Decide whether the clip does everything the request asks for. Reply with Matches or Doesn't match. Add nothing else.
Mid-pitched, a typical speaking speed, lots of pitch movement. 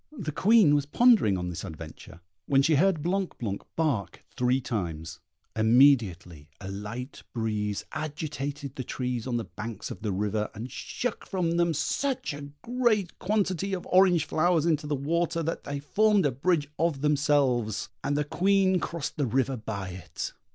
Matches